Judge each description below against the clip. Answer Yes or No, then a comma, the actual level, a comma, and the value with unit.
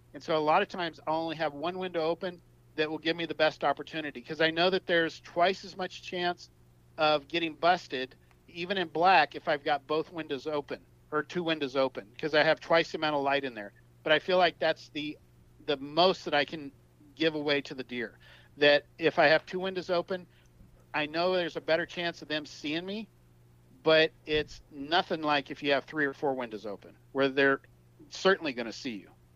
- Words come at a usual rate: No, fast, 215 wpm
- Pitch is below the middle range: No, medium, 155 Hz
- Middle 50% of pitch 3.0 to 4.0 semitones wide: Yes, average, 3.4 semitones